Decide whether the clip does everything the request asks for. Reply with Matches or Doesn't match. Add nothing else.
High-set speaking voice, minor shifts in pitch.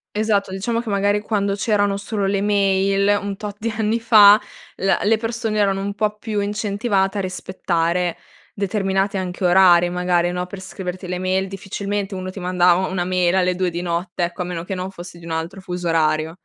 Matches